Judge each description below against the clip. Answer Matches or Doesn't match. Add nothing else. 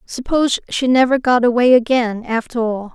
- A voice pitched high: Matches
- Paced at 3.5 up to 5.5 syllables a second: Matches